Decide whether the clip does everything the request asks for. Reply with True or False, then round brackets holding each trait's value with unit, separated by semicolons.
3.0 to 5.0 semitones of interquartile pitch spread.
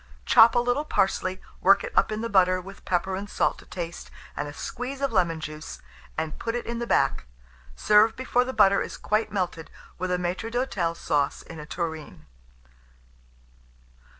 False (5.4 semitones)